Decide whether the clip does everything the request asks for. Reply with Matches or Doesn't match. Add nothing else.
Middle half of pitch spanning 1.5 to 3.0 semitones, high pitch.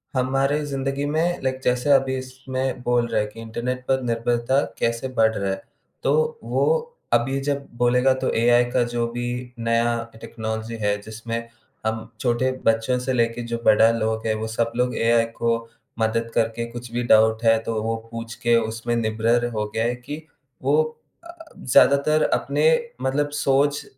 Doesn't match